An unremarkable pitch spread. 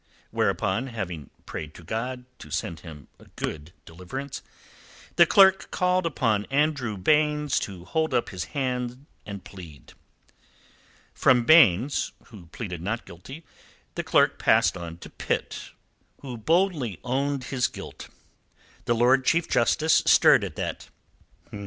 No: wide, 7.7 semitones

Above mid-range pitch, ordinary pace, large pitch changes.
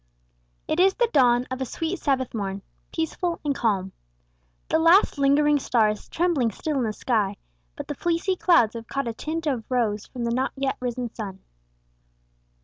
Yes: very high, 260 Hz; average, 180 wpm; wide, 5.7 semitones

